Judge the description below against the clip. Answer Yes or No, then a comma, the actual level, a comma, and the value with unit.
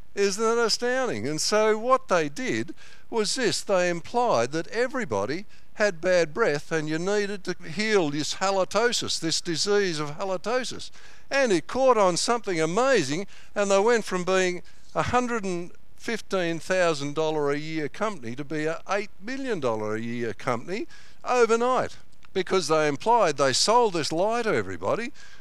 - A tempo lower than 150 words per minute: No, average, 160 wpm